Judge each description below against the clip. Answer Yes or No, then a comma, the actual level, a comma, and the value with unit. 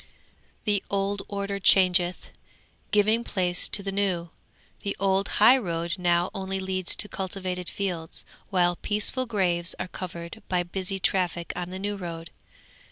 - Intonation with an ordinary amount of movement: No, narrow, 2.2 semitones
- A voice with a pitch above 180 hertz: Yes, high, 190 Hz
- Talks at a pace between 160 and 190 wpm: No, average, 145 wpm